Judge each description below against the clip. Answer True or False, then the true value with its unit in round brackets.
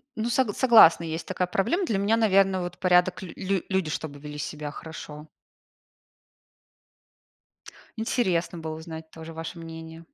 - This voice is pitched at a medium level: True (175 Hz)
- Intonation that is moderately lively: True (3.3 semitones)